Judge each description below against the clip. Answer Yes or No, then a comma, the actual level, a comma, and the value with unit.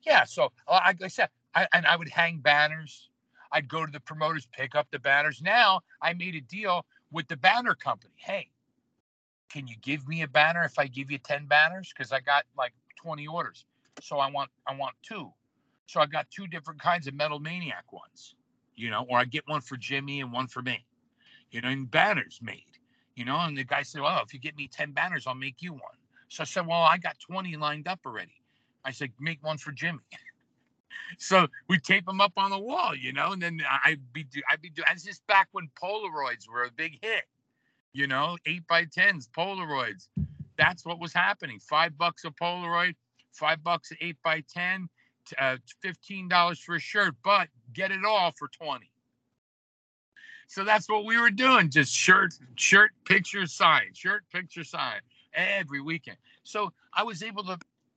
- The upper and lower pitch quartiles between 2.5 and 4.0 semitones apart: No, average, 4.5 semitones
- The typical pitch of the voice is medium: Yes, medium, 160 Hz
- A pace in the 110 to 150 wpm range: No, average, 200 wpm